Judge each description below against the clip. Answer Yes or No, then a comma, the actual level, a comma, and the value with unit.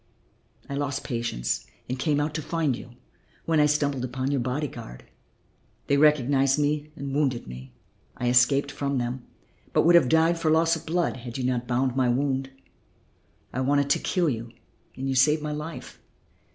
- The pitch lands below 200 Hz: Yes, medium, 140 Hz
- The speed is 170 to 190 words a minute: Yes, average, 180 wpm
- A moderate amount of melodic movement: Yes, average, 3.1 semitones